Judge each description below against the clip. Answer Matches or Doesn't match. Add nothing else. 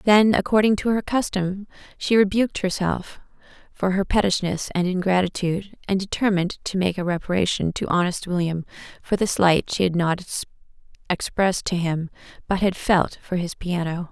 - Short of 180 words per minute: Matches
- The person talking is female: Matches